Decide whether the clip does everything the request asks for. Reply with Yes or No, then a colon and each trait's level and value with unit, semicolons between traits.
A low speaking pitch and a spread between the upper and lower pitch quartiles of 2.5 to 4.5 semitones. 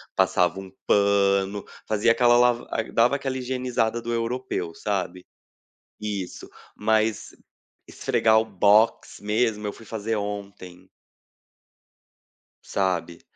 Yes: low, 105 Hz; average, 2.9 semitones